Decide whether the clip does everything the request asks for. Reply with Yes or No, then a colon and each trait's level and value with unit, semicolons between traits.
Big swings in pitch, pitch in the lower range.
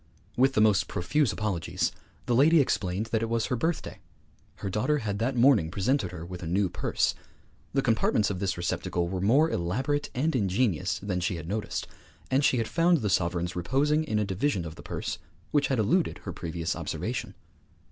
Yes: wide, 6.8 semitones; low, 105 Hz